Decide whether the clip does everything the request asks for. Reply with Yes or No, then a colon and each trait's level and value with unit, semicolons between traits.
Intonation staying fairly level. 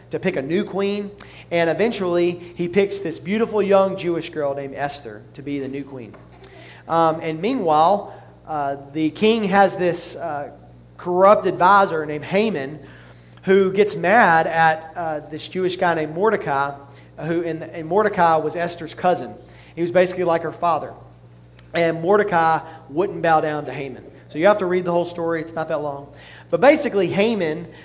No: average, 4.0 semitones